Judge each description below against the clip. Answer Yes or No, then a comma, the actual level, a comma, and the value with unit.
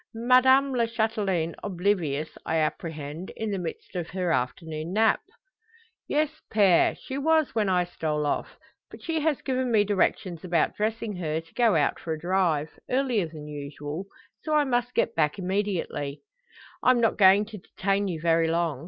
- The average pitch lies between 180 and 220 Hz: Yes, high, 190 Hz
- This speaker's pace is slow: No, average, 170 wpm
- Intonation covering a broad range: Yes, wide, 5.9 semitones